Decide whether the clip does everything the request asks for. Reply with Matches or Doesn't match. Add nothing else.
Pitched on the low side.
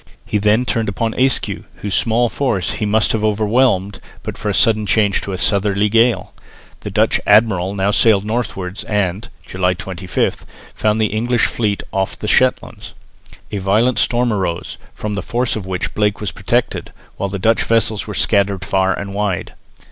Matches